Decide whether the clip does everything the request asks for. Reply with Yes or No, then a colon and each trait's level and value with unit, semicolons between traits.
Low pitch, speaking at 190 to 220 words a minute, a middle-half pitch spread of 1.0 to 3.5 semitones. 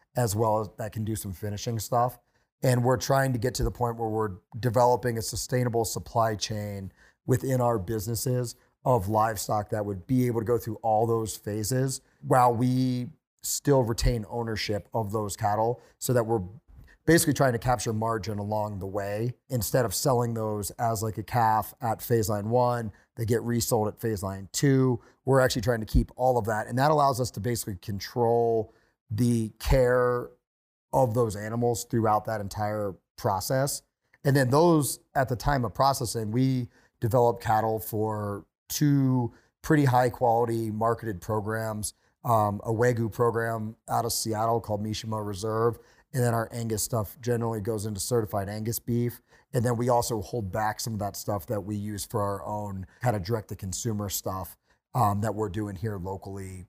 No: low, 115 Hz; average, 175 wpm; narrow, 2.5 semitones